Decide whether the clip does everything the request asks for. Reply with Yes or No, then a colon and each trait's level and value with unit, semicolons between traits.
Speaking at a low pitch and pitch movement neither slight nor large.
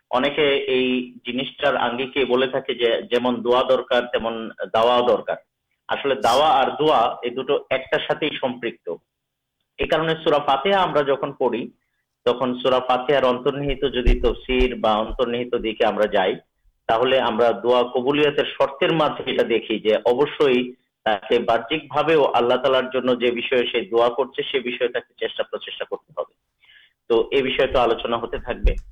Yes: low, 130 Hz; average, 3.2 semitones